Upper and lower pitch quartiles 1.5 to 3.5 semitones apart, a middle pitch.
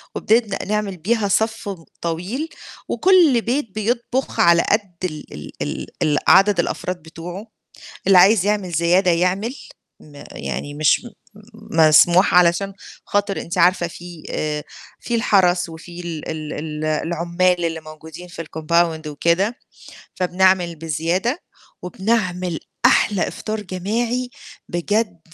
No: average, 3.9 semitones; medium, 180 Hz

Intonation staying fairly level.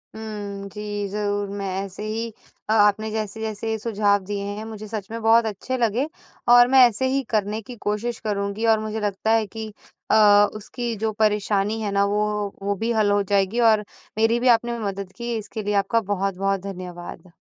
Yes: narrow, 1.8 semitones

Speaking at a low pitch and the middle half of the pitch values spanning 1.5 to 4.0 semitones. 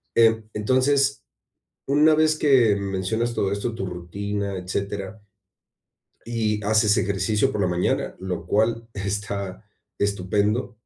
Yes: low, 105 Hz; average, 2.8 semitones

